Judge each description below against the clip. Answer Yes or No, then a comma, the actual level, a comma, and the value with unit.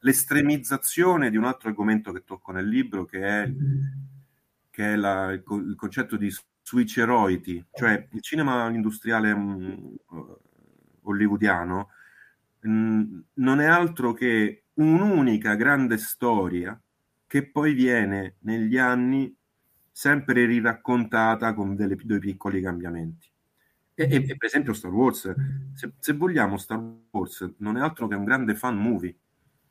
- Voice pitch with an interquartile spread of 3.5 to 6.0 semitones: Yes, average, 5.2 semitones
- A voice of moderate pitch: No, low, 115 Hz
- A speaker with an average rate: Yes, average, 130 wpm